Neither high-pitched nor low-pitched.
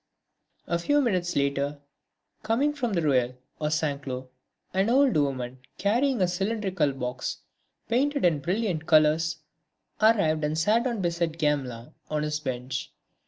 Yes: medium, 160 Hz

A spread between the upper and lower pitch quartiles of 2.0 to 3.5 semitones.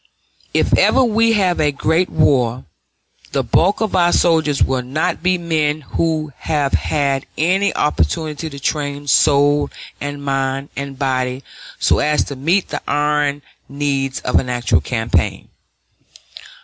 Yes: average, 2.9 semitones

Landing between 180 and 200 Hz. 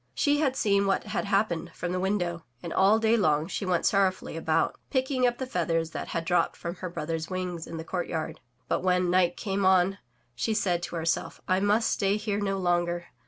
Yes: medium, 185 Hz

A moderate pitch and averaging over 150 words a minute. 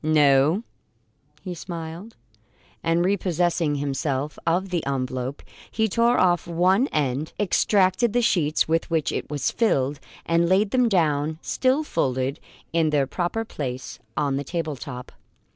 No: medium, 165 Hz; average, 140 wpm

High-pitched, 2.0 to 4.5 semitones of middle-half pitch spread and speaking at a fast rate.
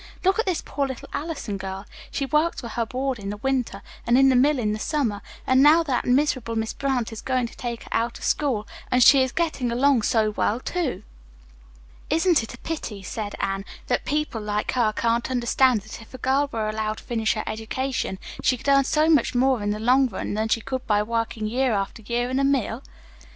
Yes: high, 245 Hz; average, 3.8 semitones; fast, 225 wpm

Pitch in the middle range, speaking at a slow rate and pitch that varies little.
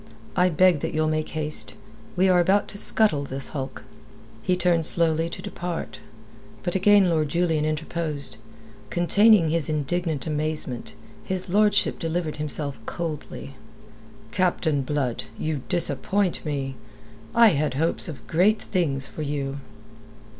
No: medium, 160 Hz; slow, 130 wpm; average, 3.5 semitones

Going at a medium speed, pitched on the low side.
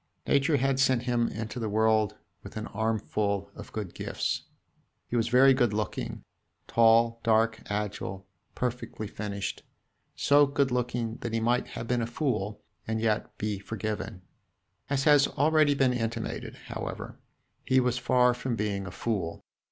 Yes: average, 150 wpm; low, 115 Hz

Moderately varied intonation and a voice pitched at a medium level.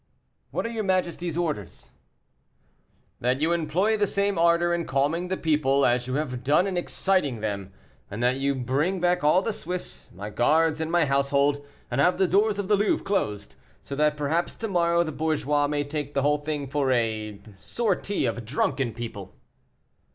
Yes: average, 4.9 semitones; medium, 150 Hz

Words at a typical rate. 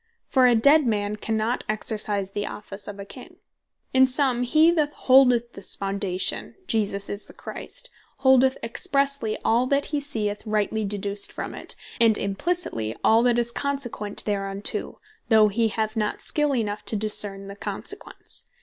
Yes: average, 160 wpm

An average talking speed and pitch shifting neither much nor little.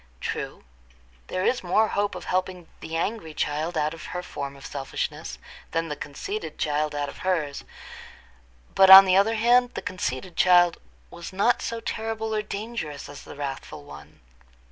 No: average, 165 wpm; wide, 5.9 semitones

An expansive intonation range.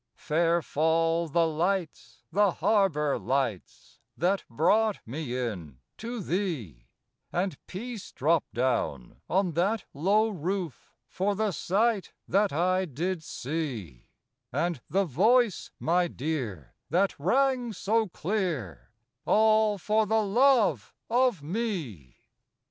Yes: wide, 6.1 semitones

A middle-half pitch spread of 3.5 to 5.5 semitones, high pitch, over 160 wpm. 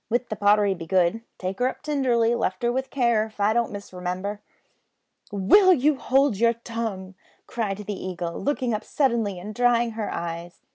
Yes: average, 3.9 semitones; high, 220 Hz; average, 180 wpm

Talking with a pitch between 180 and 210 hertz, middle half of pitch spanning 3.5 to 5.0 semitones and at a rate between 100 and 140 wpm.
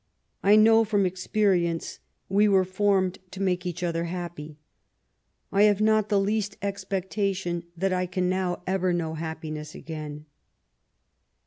No: medium, 185 Hz; narrow, 2.6 semitones; slow, 135 wpm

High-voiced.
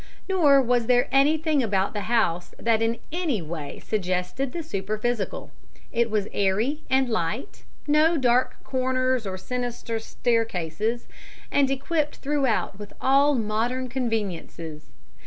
Yes: high, 240 Hz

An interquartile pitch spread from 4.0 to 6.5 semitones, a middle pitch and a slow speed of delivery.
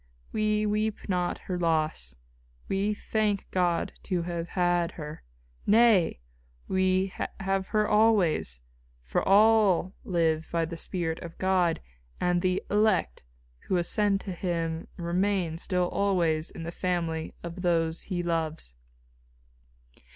No: average, 2.9 semitones; medium, 180 Hz; slow, 125 wpm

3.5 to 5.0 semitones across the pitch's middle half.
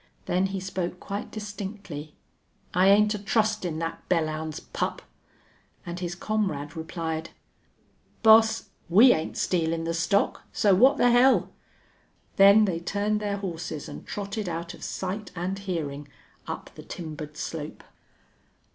Yes: average, 3.9 semitones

